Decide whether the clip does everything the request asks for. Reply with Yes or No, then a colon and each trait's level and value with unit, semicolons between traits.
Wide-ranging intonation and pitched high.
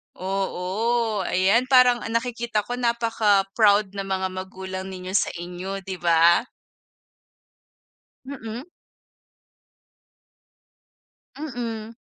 No: average, 3.8 semitones; high, 205 Hz